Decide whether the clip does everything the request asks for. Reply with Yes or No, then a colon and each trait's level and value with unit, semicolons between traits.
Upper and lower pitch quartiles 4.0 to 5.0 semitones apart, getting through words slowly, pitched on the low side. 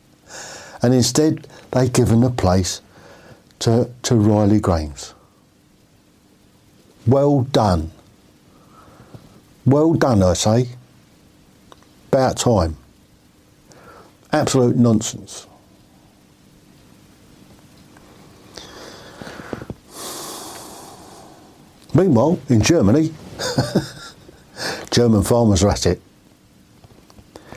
Yes: average, 4.6 semitones; slow, 65 wpm; low, 115 Hz